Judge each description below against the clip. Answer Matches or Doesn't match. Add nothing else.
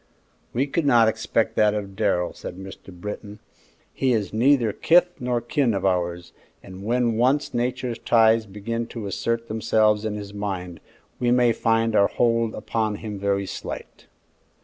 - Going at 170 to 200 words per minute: Doesn't match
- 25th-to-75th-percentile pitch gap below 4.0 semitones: Matches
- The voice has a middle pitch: Doesn't match